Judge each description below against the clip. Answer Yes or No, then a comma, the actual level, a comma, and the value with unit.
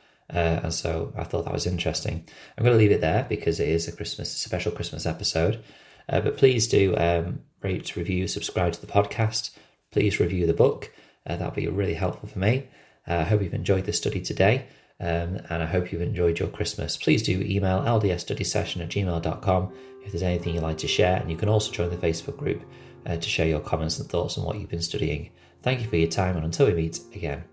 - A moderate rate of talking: No, fast, 225 wpm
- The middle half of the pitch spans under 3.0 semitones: No, average, 3.7 semitones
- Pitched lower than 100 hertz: Yes, very low, 90 Hz